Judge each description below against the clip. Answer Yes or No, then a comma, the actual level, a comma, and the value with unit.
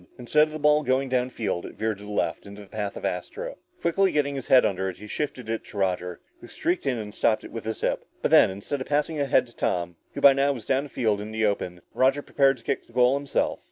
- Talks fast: Yes, fast, 275 wpm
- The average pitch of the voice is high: No, low, 125 Hz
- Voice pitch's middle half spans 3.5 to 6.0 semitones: Yes, average, 5.3 semitones